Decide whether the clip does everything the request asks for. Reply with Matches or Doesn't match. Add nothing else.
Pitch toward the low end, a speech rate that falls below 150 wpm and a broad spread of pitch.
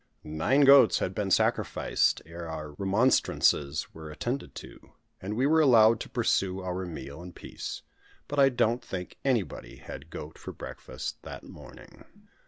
Doesn't match